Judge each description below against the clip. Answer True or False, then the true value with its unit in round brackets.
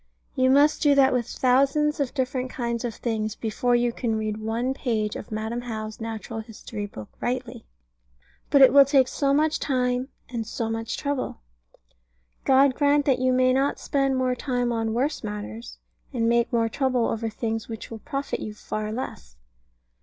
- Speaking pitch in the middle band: False (245 Hz)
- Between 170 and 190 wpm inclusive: True (175 wpm)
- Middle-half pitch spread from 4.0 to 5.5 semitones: False (3.1 semitones)